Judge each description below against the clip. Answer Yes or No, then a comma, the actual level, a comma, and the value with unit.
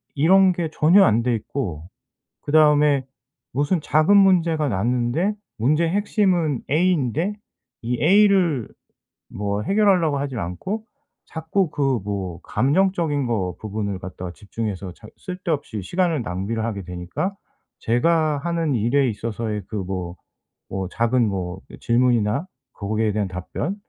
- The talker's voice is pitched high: No, low, 130 Hz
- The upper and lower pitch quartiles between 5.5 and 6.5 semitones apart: No, wide, 8.2 semitones